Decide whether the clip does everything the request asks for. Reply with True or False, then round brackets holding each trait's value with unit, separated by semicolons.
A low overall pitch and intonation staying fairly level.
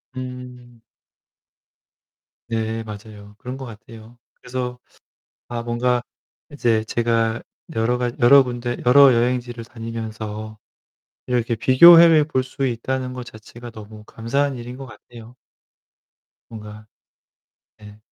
True (120 Hz; 2.1 semitones)